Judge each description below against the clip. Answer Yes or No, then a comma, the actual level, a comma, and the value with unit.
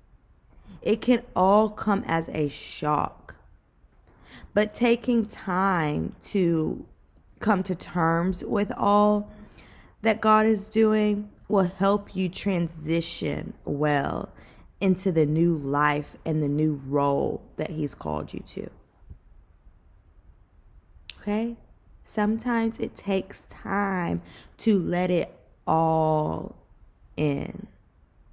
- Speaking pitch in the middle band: Yes, medium, 170 Hz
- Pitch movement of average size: No, wide, 6.6 semitones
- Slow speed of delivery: Yes, slow, 100 wpm